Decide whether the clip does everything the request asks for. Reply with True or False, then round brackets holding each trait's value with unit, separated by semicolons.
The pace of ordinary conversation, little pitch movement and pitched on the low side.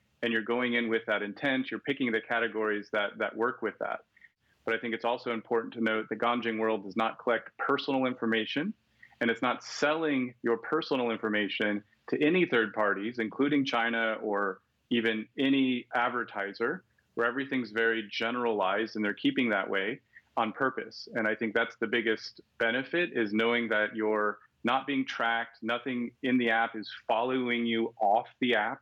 True (175 wpm; 2.1 semitones; 115 Hz)